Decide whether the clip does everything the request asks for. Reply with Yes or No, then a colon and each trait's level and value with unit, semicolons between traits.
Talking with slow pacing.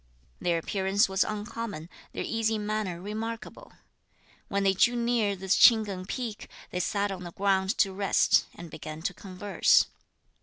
No: average, 155 wpm